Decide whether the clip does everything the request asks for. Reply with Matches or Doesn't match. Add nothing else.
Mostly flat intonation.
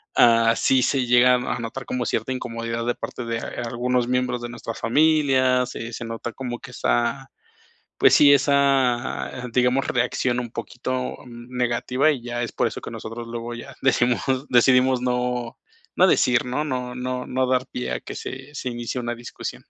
Matches